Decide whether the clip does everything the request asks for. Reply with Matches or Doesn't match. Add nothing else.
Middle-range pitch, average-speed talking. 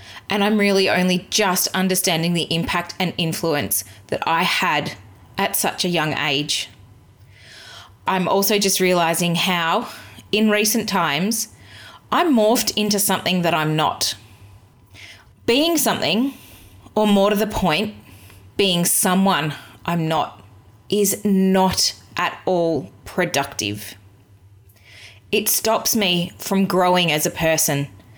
Doesn't match